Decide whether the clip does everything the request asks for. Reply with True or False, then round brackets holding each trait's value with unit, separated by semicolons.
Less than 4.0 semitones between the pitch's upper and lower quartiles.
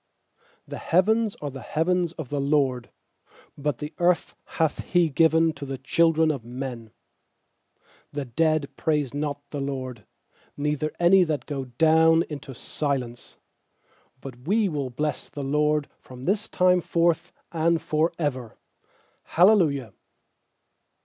True (3.4 semitones)